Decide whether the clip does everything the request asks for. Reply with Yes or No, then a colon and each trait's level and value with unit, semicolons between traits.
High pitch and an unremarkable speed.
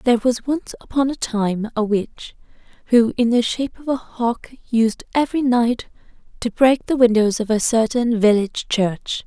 Yes: high, 235 Hz; average, 175 wpm